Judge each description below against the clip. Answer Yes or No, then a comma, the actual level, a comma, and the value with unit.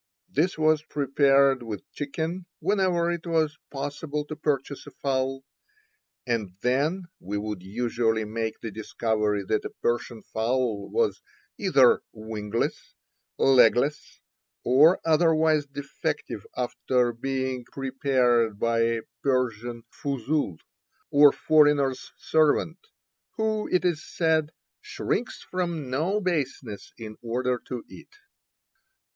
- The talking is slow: Yes, slow, 110 wpm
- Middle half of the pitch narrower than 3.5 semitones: No, average, 5.1 semitones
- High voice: No, low, 135 Hz